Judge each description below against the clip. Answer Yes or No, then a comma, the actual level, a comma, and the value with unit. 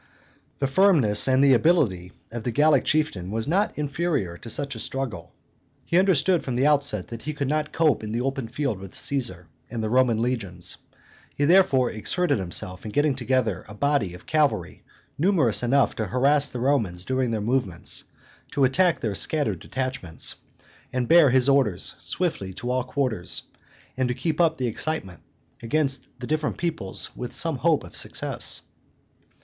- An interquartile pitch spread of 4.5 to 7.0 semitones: Yes, average, 5.2 semitones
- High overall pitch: No, low, 130 Hz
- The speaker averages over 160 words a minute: Yes, average, 170 wpm